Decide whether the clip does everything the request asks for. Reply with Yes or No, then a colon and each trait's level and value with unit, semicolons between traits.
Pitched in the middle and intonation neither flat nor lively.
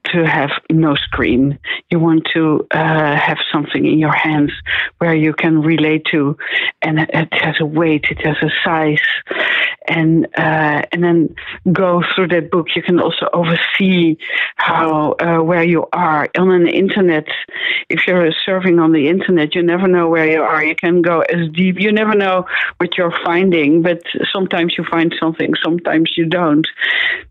No: medium, 165 Hz; narrow, 2.0 semitones